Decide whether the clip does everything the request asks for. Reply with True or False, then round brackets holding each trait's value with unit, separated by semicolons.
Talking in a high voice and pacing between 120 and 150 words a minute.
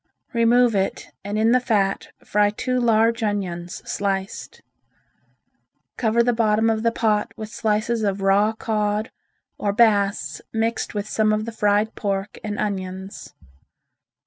True (215 Hz; 140 wpm)